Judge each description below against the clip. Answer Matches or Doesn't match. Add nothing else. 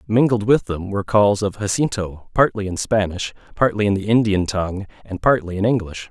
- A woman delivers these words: Doesn't match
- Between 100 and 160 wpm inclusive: Doesn't match